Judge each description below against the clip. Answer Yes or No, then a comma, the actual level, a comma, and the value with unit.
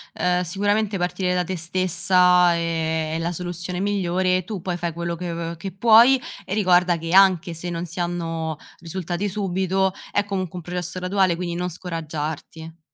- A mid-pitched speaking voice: Yes, medium, 180 Hz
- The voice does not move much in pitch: Yes, narrow, 1.8 semitones